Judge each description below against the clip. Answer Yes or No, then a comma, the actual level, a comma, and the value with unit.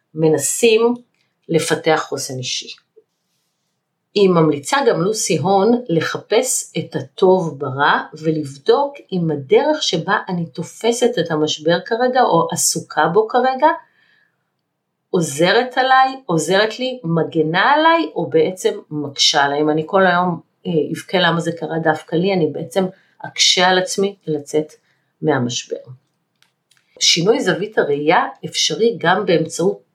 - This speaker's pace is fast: No, average, 120 wpm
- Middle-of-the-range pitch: Yes, medium, 170 Hz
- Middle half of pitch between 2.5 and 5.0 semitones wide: No, wide, 5.6 semitones